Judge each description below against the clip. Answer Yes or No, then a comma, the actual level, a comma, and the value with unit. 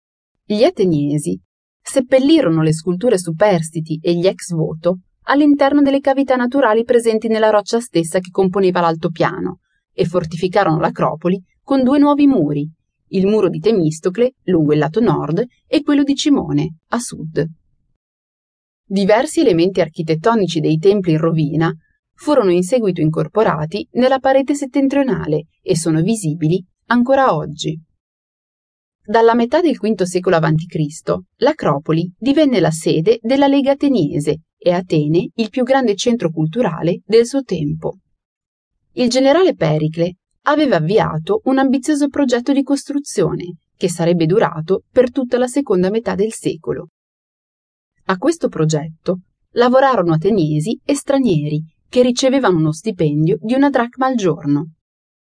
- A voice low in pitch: No, high, 195 Hz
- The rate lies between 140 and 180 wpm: No, average, 130 wpm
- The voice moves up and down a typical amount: No, wide, 7.9 semitones